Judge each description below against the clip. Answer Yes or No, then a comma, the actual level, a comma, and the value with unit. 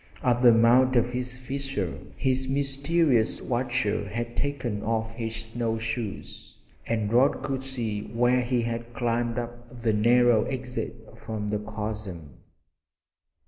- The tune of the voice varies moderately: No, narrow, 2.3 semitones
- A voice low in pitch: Yes, low, 120 Hz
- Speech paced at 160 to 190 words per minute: No, slow, 135 wpm